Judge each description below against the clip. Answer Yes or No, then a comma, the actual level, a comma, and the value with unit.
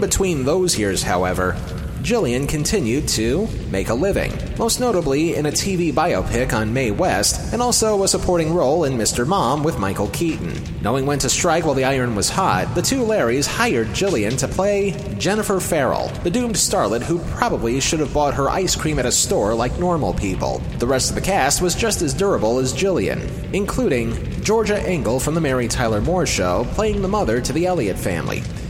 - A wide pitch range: Yes, wide, 7.3 semitones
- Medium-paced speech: Yes, average, 190 wpm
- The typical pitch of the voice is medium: Yes, medium, 150 Hz